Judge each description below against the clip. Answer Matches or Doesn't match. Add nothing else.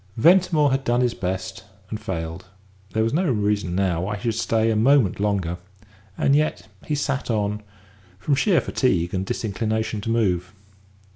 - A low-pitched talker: Matches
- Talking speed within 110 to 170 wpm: Matches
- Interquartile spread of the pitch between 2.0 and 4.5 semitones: Doesn't match